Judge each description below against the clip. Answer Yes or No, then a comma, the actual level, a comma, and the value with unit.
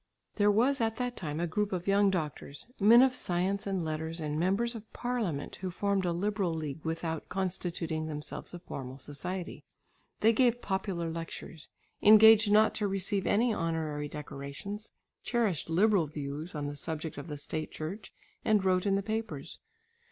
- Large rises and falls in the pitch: No, average, 4.8 semitones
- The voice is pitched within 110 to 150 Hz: No, medium, 180 Hz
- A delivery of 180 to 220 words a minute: No, average, 165 wpm